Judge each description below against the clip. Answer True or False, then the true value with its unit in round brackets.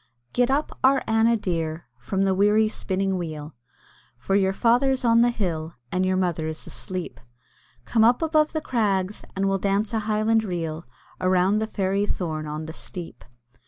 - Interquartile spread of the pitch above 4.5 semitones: False (4.1 semitones)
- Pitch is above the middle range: True (195 Hz)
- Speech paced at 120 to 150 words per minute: False (170 wpm)